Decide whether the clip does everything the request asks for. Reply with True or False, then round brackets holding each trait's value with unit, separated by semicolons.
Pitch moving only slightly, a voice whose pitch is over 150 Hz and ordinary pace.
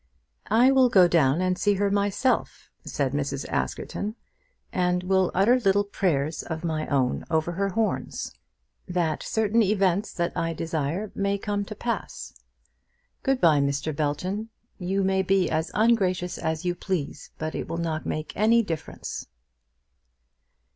False (4.2 semitones; 185 Hz; 150 wpm)